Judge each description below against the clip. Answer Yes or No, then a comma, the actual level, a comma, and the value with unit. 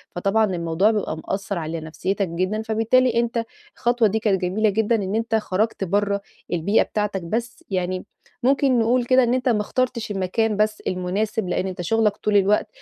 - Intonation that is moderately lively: Yes, average, 3.3 semitones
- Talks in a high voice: Yes, high, 210 Hz